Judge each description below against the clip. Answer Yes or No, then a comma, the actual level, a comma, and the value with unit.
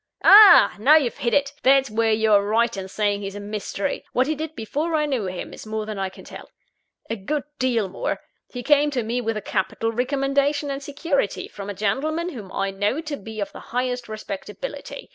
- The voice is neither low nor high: No, high, 235 Hz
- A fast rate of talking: Yes, fast, 210 wpm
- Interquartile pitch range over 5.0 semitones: Yes, wide, 5.5 semitones